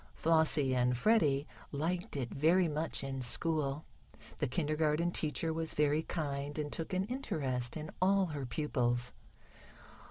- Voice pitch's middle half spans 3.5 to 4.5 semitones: No, average, 3.1 semitones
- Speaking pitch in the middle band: Yes, medium, 150 Hz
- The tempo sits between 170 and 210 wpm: No, slow, 135 wpm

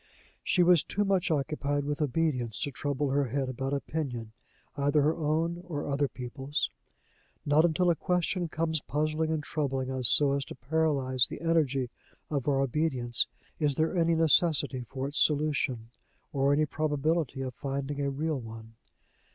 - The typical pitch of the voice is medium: Yes, medium, 145 Hz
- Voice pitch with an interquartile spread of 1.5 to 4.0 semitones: Yes, average, 2.9 semitones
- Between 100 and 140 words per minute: No, average, 160 wpm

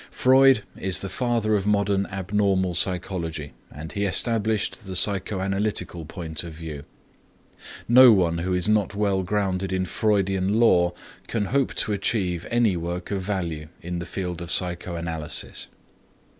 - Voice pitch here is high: No, very low, 95 Hz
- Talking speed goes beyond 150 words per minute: No, average, 145 wpm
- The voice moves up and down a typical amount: Yes, average, 3.1 semitones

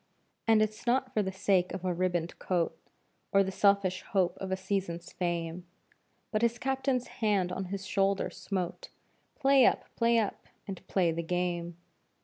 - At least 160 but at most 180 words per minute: Yes, average, 165 wpm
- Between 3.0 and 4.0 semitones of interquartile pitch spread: Yes, average, 3.3 semitones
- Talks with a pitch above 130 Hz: Yes, high, 190 Hz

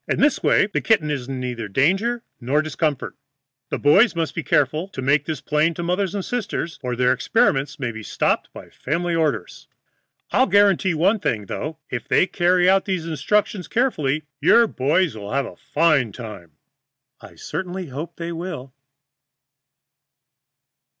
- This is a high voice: No, medium, 155 Hz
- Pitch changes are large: Yes, wide, 5.8 semitones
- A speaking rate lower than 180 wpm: Yes, average, 165 wpm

